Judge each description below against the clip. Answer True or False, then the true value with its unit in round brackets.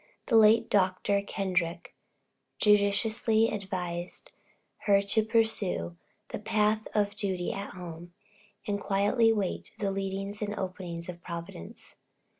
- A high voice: True (200 Hz)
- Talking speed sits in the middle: False (115 wpm)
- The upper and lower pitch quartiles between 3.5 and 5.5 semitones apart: False (2.7 semitones)